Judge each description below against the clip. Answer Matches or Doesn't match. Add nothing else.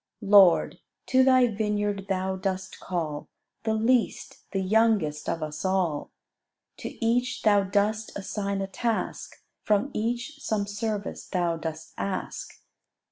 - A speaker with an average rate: Doesn't match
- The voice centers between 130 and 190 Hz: Doesn't match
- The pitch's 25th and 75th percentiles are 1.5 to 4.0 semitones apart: Matches